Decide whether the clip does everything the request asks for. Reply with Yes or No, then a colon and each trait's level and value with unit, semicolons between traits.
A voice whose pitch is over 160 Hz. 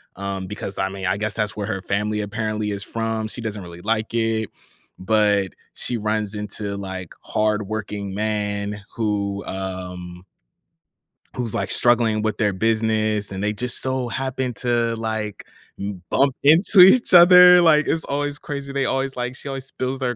No: low, 110 Hz